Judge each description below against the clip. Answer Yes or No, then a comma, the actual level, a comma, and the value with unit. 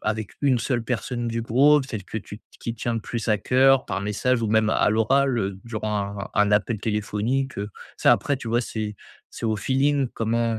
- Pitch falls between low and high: No, low, 115 Hz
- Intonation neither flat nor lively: Yes, average, 3.1 semitones